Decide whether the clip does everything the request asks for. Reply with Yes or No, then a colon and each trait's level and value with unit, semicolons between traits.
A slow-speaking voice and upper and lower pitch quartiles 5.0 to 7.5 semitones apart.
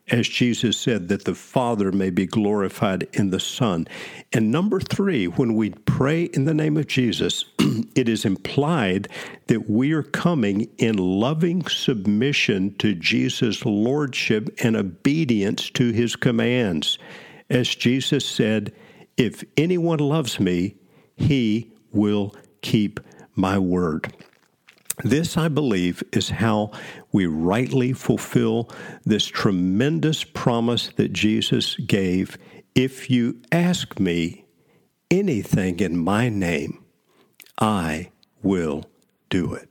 Yes: slow, 120 wpm; wide, 5.6 semitones